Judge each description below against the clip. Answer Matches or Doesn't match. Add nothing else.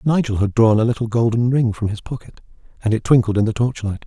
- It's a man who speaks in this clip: Matches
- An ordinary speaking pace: Doesn't match